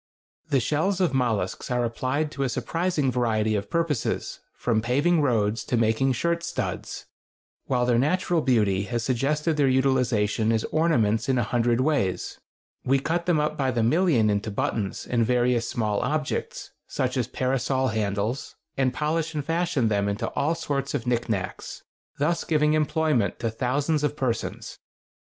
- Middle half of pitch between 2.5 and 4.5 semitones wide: No, average, 4.9 semitones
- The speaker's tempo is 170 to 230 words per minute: No, average, 160 wpm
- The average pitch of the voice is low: Yes, low, 130 Hz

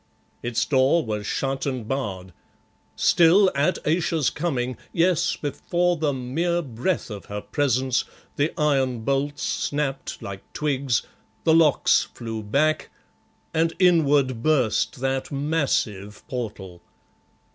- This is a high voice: No, low, 135 Hz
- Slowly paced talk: Yes, slow, 115 wpm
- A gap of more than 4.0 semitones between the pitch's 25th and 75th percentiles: Yes, average, 4.5 semitones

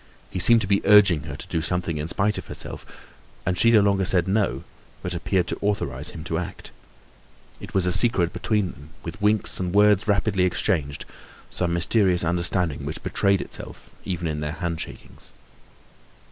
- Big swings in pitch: No, average, 3.2 semitones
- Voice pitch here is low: Yes, very low, 90 Hz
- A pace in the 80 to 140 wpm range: No, average, 180 wpm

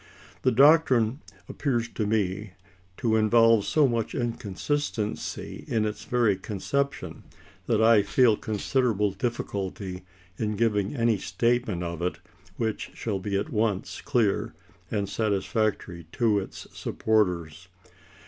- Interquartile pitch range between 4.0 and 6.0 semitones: No, average, 3.1 semitones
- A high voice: No, low, 110 Hz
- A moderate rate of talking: No, slow, 120 wpm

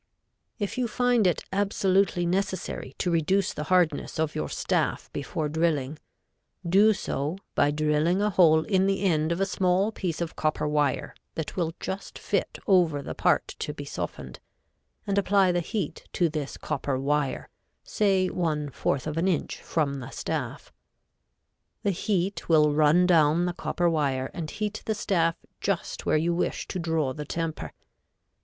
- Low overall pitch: No, medium, 170 Hz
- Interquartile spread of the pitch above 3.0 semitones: Yes, average, 4.0 semitones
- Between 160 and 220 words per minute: Yes, average, 165 wpm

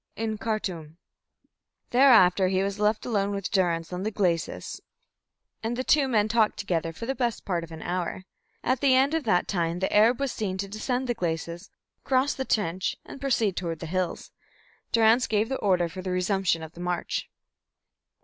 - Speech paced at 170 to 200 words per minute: Yes, average, 190 wpm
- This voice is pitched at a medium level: No, high, 200 Hz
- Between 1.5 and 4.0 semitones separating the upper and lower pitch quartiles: No, average, 4.5 semitones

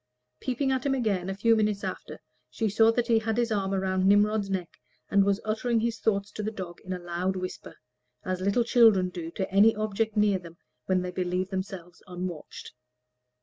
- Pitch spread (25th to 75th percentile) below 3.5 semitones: Yes, average, 3.1 semitones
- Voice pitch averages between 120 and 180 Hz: No, high, 200 Hz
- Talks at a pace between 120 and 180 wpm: No, average, 195 wpm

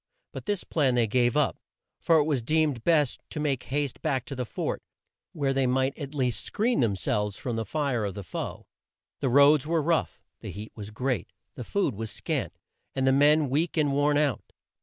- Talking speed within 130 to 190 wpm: No, fast, 205 wpm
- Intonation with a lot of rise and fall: No, average, 3.8 semitones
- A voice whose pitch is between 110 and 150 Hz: Yes, low, 135 Hz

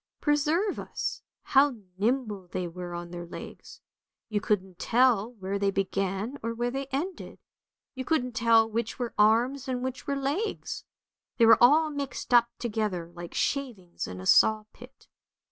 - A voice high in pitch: Yes, high, 230 Hz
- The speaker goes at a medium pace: Yes, average, 160 wpm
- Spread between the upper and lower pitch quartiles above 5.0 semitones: Yes, wide, 5.4 semitones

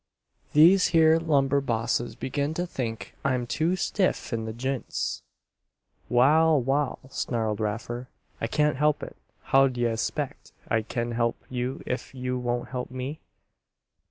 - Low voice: Yes, low, 130 Hz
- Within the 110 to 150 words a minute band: Yes, average, 140 wpm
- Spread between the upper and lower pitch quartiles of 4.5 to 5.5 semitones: No, average, 3.7 semitones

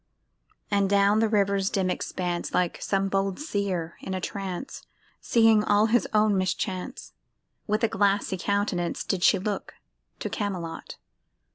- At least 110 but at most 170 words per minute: Yes, average, 140 wpm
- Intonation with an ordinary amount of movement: No, narrow, 2.1 semitones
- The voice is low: No, high, 200 Hz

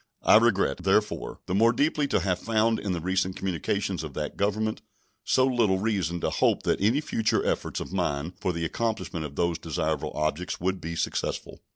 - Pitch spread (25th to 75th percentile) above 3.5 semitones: Yes, average, 4.7 semitones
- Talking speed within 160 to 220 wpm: Yes, average, 190 wpm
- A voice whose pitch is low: Yes, very low, 95 Hz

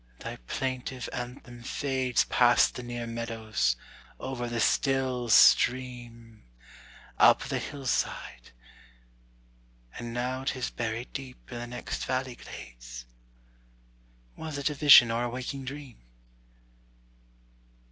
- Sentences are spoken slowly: Yes, slow, 110 wpm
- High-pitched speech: No, low, 125 Hz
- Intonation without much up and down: Yes, narrow, 1.9 semitones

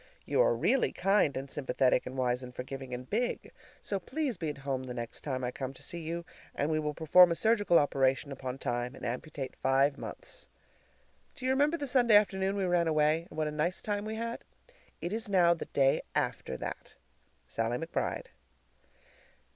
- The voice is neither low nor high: Yes, medium, 155 Hz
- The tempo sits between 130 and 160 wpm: No, average, 195 wpm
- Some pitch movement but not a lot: No, wide, 7.1 semitones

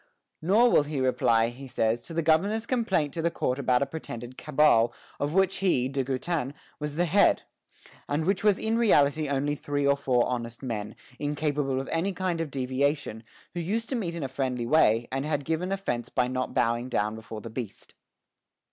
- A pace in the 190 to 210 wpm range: Yes, average, 195 wpm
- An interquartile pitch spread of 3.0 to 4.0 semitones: No, average, 4.9 semitones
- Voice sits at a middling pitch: Yes, medium, 145 Hz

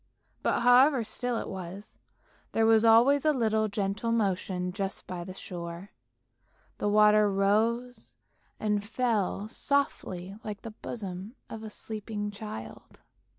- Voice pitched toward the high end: Yes, high, 210 Hz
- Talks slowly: Yes, slow, 130 wpm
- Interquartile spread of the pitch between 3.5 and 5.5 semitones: No, average, 2.8 semitones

